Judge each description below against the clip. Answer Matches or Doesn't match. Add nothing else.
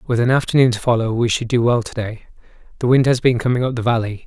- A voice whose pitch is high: Doesn't match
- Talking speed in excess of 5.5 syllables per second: Matches